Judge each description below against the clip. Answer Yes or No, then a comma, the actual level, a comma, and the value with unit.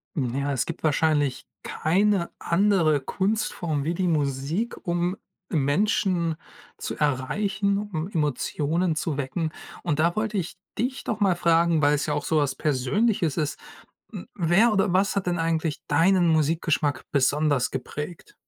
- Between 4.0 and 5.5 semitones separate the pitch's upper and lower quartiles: Yes, average, 4.4 semitones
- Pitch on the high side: No, medium, 165 Hz